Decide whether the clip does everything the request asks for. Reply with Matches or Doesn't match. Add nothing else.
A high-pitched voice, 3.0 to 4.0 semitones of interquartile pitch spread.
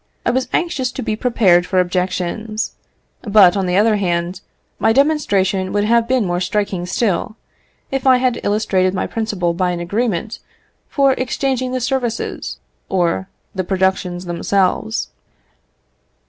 Doesn't match